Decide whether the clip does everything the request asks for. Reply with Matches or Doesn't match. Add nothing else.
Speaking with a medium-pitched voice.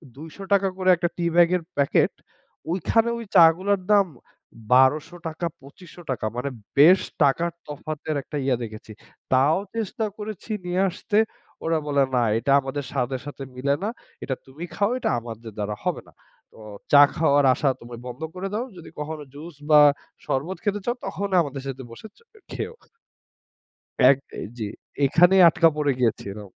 Matches